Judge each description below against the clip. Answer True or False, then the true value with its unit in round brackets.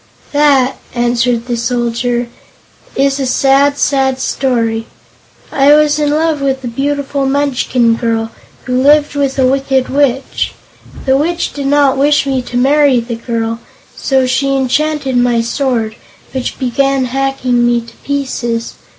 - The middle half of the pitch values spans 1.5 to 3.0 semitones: True (2.6 semitones)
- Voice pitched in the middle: False (265 Hz)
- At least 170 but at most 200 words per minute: False (140 wpm)